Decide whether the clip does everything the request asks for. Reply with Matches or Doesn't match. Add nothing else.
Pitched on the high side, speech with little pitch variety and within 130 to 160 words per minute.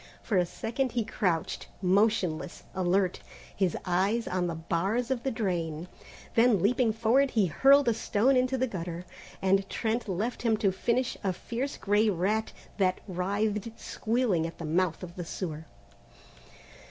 Doesn't match